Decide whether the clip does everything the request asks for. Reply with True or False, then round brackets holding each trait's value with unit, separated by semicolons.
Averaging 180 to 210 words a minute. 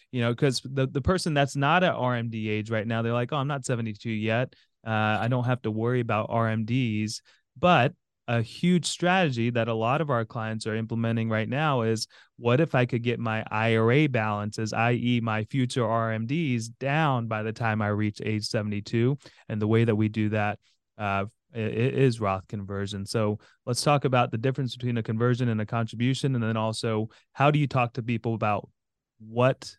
True (200 wpm)